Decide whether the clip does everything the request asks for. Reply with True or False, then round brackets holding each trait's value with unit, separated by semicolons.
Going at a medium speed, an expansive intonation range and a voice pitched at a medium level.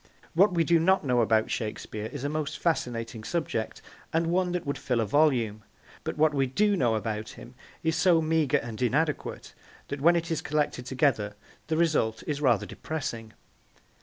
True (180 wpm; 5.9 semitones; 145 Hz)